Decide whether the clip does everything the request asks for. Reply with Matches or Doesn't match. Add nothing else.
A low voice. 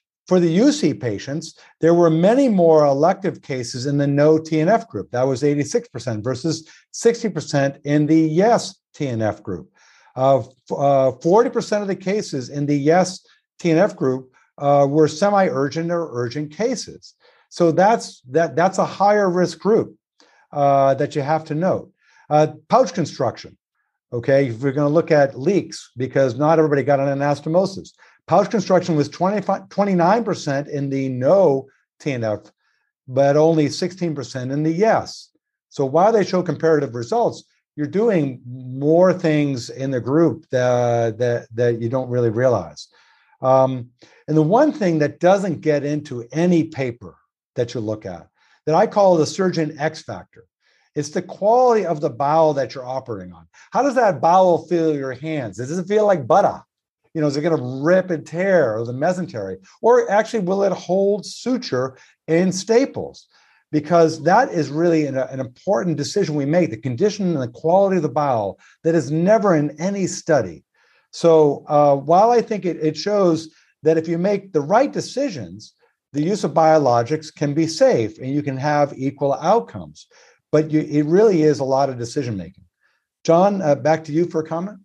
Doesn't match